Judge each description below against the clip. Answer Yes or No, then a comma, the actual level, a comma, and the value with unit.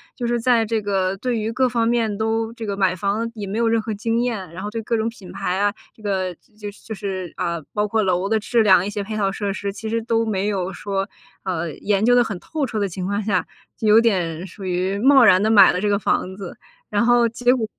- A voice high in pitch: Yes, high, 210 Hz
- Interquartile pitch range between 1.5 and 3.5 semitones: Yes, average, 2.9 semitones